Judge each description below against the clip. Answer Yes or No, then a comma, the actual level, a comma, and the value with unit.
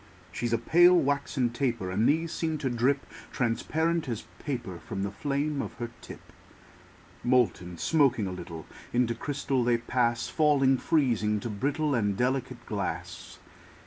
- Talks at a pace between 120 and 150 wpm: Yes, average, 145 wpm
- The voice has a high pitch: No, low, 125 Hz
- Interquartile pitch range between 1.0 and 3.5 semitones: No, average, 3.9 semitones